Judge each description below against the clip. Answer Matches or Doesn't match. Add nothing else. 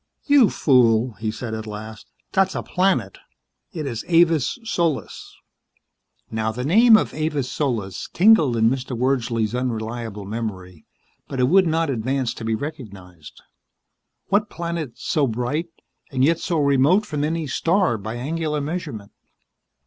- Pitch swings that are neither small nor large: Doesn't match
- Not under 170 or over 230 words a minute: Doesn't match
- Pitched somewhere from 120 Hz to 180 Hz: Matches